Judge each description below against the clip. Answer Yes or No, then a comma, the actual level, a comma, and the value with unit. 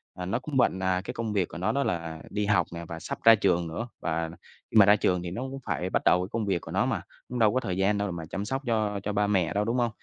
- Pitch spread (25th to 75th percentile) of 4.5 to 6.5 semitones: No, average, 4.0 semitones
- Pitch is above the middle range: No, low, 100 Hz